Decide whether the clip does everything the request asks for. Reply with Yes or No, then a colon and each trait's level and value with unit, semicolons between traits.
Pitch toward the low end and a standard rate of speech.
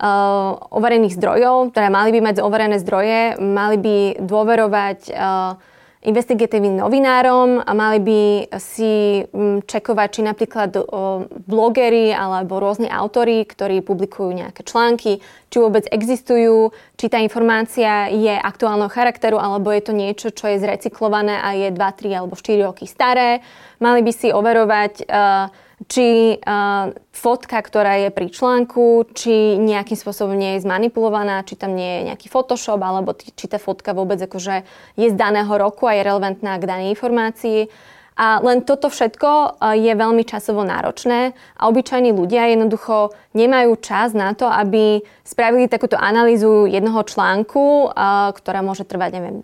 No: high, 215 Hz; average, 150 wpm